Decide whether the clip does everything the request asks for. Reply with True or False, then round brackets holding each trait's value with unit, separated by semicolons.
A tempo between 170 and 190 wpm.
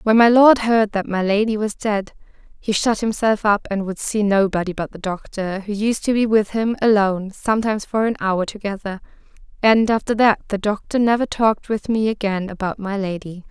False (200 wpm)